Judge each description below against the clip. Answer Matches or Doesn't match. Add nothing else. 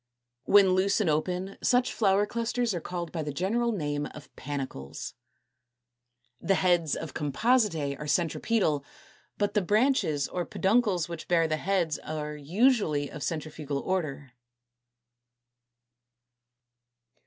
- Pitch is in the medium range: Matches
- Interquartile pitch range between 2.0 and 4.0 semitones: Doesn't match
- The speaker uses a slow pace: Matches